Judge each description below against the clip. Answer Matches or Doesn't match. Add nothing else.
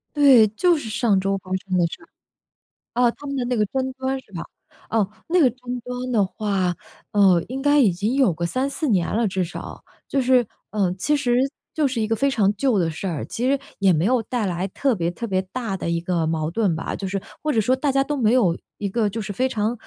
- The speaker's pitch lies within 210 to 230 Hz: Matches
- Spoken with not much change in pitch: Doesn't match